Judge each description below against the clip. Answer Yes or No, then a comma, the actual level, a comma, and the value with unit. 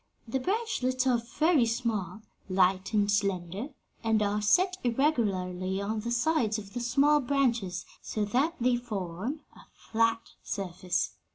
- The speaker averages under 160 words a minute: Yes, slow, 135 wpm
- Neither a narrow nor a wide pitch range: Yes, average, 4.6 semitones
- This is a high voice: Yes, high, 225 Hz